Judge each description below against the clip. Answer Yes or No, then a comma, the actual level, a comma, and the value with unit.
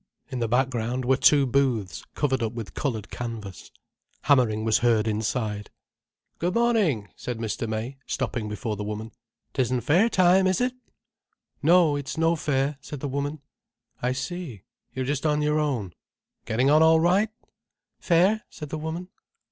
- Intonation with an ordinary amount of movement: No, wide, 5.9 semitones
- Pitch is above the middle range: No, low, 135 Hz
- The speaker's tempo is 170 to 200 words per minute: No, average, 155 wpm